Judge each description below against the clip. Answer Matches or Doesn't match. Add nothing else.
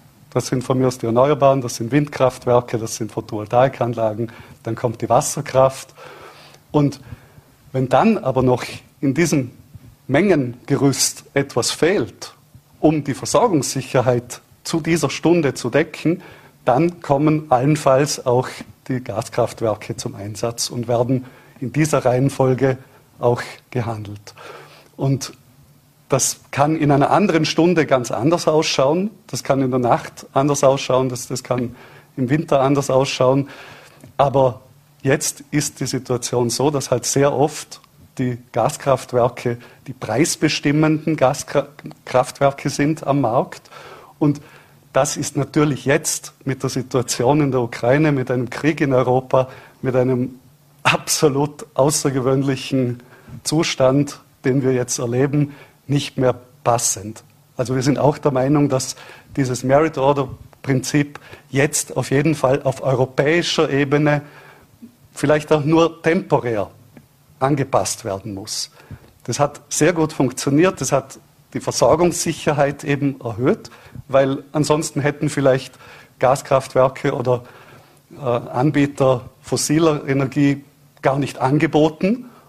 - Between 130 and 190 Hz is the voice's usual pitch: Matches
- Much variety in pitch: Doesn't match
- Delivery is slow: Matches